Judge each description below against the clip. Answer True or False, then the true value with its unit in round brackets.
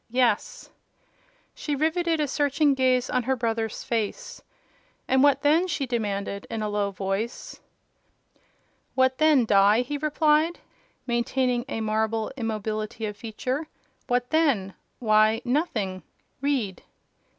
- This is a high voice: True (245 Hz)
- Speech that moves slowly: True (115 wpm)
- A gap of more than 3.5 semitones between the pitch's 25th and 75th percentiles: True (4.8 semitones)